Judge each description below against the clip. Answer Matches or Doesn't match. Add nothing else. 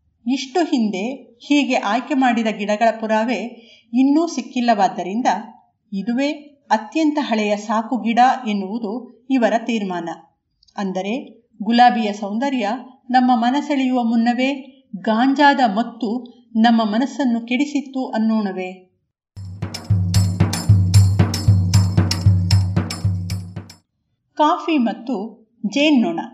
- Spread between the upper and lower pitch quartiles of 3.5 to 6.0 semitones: Matches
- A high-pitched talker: Matches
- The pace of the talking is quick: Doesn't match